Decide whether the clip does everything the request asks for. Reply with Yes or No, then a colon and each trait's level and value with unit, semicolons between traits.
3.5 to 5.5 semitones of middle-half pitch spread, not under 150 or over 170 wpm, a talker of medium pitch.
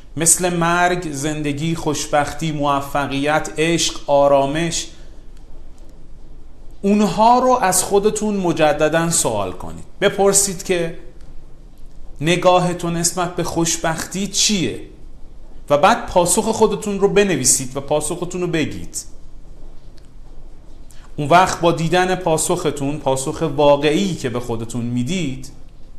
No: average, 3.9 semitones; slow, 95 wpm; medium, 165 Hz